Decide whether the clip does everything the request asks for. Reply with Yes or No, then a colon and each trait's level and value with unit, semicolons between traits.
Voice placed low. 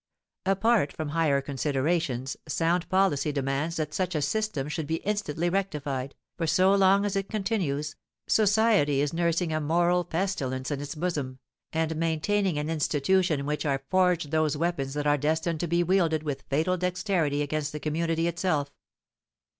No: medium, 160 Hz